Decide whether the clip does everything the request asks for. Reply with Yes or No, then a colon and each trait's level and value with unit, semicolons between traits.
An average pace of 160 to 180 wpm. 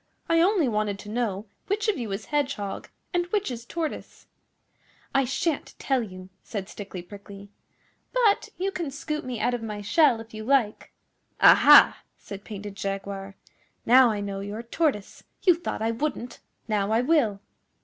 Yes: average, 165 wpm